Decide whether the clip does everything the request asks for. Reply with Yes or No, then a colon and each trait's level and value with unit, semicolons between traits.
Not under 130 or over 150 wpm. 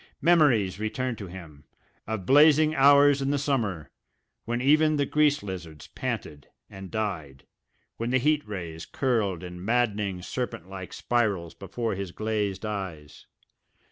Yes: average, 140 wpm